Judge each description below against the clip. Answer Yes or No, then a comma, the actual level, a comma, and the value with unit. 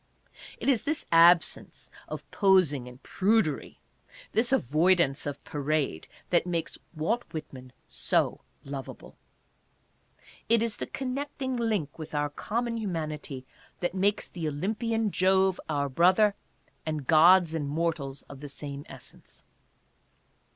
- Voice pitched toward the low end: No, medium, 170 Hz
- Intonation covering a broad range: Yes, wide, 6.2 semitones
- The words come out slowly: Yes, slow, 125 wpm